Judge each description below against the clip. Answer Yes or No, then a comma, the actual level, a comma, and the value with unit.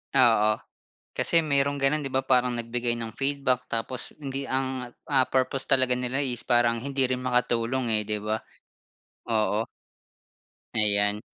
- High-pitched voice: No, low, 125 Hz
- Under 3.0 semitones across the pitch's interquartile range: Yes, narrow, 2.5 semitones